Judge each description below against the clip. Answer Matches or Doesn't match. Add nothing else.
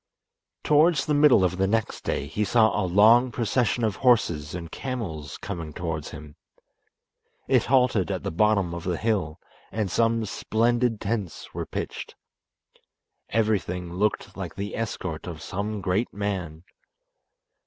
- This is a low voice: Matches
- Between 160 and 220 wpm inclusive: Doesn't match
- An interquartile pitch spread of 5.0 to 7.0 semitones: Doesn't match